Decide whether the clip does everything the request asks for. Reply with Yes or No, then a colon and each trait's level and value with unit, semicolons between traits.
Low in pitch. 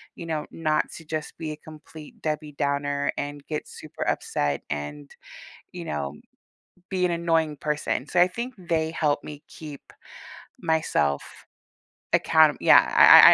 No: medium, 155 Hz